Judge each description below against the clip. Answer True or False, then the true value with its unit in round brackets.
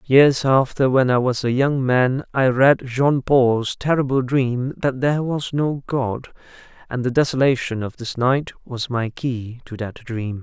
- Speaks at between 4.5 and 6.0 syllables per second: False (4.0 syllables/s)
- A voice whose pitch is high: False (130 Hz)